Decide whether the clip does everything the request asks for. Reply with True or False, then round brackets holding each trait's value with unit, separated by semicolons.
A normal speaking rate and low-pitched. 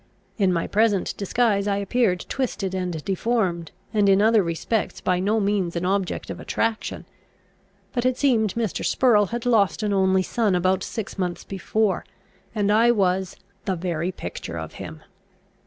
False (160 wpm; 200 Hz)